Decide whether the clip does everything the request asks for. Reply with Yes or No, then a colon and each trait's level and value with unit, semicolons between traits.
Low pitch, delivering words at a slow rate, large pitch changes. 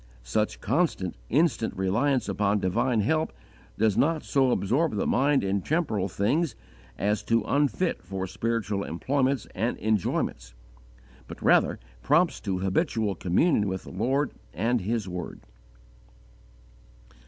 Yes: low, 110 Hz; slow, 125 wpm; wide, 6.0 semitones